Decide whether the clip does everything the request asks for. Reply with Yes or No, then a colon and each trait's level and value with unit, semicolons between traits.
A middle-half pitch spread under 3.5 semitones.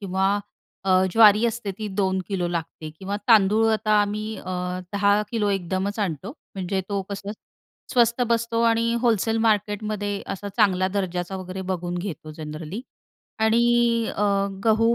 Yes: average, 2.8 semitones